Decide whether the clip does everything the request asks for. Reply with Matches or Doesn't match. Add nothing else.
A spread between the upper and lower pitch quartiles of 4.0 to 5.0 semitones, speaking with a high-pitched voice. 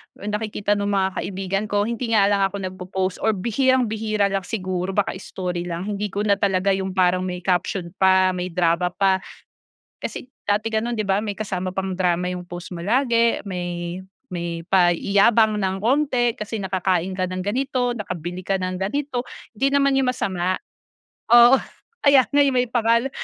Doesn't match